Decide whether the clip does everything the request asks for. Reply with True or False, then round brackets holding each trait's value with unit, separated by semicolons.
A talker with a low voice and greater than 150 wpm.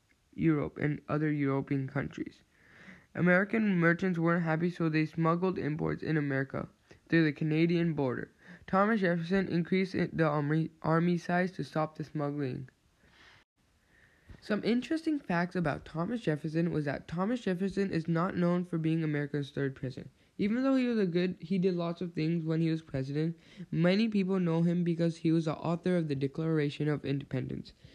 False (165 Hz; 165 wpm)